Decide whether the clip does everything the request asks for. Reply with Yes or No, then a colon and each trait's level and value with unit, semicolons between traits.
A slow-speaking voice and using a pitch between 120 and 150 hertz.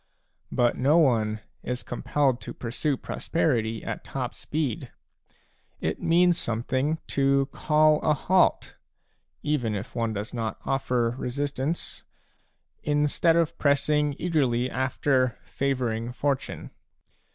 Yes: slow, 125 wpm; low, 135 Hz